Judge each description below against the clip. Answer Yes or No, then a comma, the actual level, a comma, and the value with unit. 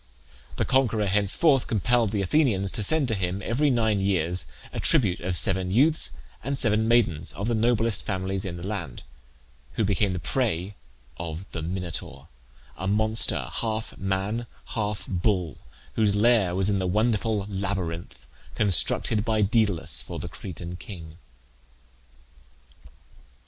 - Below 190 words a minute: Yes, average, 140 wpm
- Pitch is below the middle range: Yes, low, 100 Hz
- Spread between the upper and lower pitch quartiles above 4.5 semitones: No, average, 3.6 semitones